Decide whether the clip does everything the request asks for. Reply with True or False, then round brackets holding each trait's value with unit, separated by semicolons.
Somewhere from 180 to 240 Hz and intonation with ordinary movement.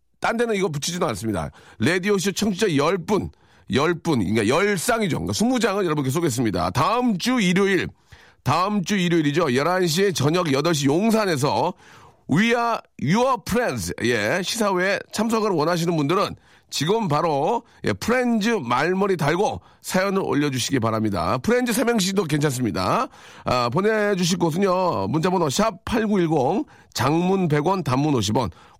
False (185 Hz; 6.1 semitones)